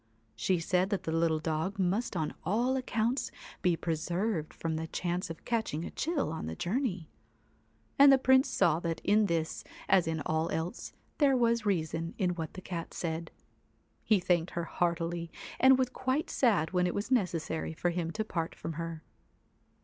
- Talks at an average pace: Yes, average, 180 wpm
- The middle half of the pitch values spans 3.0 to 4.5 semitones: No, average, 5.1 semitones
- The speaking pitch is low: No, medium, 175 Hz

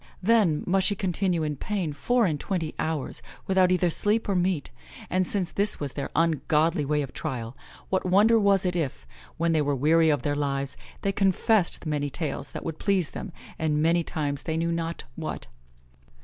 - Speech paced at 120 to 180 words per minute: No, average, 190 wpm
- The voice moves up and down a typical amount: Yes, average, 4.1 semitones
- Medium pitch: Yes, medium, 165 Hz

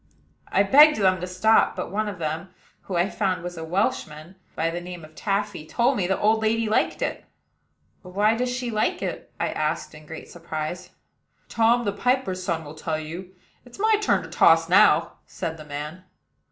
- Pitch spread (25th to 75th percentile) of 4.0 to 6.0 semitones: Yes, average, 5.1 semitones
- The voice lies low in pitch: No, medium, 185 Hz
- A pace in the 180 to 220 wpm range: Yes, average, 200 wpm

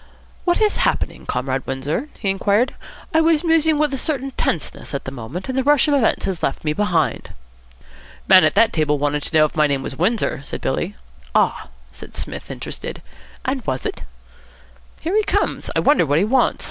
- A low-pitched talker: No, high, 195 Hz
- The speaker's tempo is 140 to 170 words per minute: No, average, 200 wpm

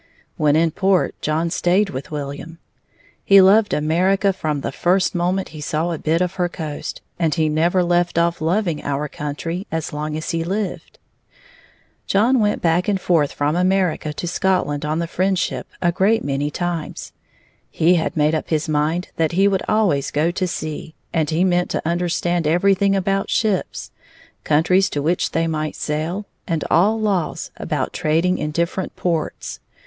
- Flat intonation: No, average, 3.3 semitones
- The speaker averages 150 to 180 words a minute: Yes, average, 170 wpm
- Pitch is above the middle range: No, medium, 170 Hz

